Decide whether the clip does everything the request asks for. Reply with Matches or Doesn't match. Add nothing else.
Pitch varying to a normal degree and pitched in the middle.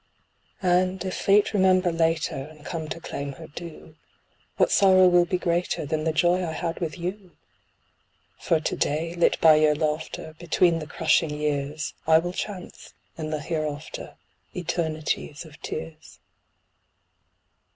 Doesn't match